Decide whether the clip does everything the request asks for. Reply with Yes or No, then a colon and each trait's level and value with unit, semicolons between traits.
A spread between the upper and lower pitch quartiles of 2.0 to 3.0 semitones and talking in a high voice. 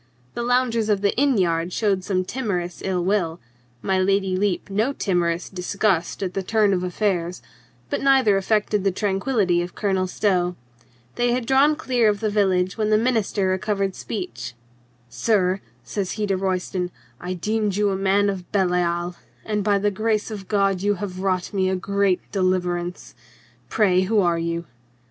Yes: average, 2.7 semitones; high, 195 Hz